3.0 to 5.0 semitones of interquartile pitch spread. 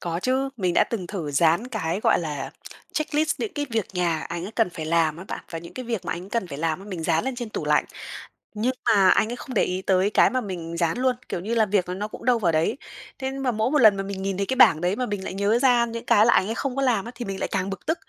No: wide, 5.4 semitones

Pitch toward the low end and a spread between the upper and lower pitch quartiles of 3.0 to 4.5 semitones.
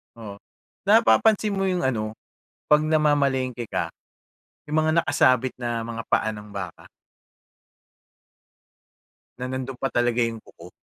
No: low, 130 Hz; average, 4.9 semitones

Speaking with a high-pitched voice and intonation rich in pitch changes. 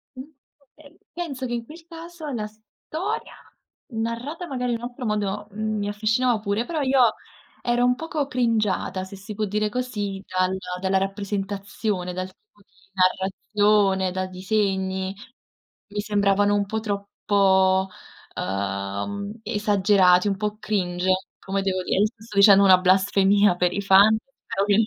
No: high, 205 Hz; average, 2.8 semitones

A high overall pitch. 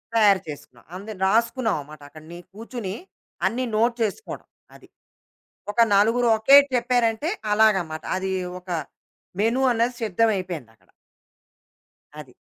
Yes: high, 215 Hz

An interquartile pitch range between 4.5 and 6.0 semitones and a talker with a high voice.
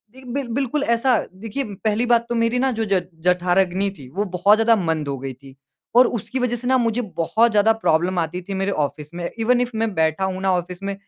Yes: average, 5.0 semitones; high, 205 Hz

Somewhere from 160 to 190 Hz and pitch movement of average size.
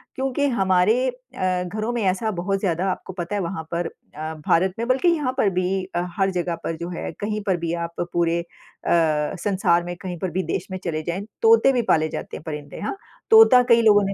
Yes: medium, 185 Hz; average, 4.0 semitones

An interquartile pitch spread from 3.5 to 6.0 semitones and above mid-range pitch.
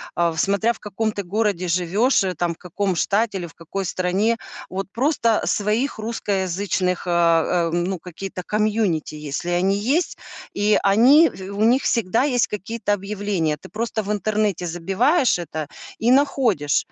Yes: average, 4.0 semitones; high, 200 Hz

